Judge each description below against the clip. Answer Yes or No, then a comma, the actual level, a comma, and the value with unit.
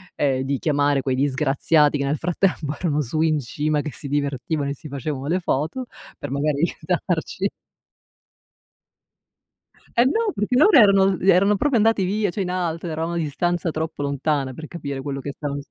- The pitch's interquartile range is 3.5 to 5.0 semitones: Yes, average, 4.2 semitones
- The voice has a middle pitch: Yes, medium, 155 Hz